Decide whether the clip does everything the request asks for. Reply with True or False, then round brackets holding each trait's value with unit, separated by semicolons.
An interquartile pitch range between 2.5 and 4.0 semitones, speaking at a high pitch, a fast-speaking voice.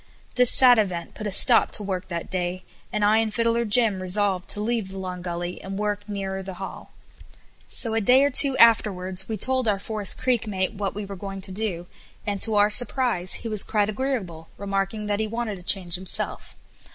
True (2.9 semitones; 205 Hz; 210 wpm)